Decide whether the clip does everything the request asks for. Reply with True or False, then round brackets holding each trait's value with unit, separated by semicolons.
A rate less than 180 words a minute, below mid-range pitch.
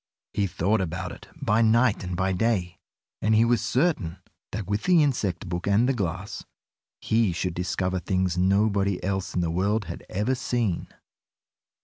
True (165 wpm; 100 Hz)